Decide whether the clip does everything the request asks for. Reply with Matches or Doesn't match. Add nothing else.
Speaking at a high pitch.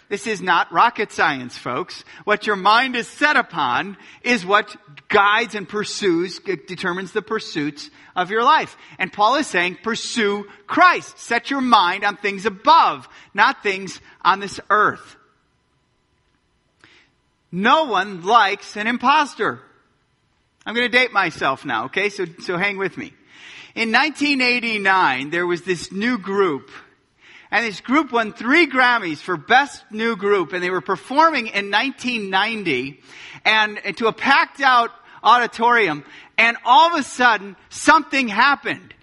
Matches